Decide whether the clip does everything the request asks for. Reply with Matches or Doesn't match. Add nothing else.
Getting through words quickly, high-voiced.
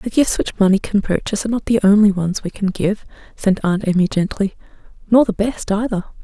Matches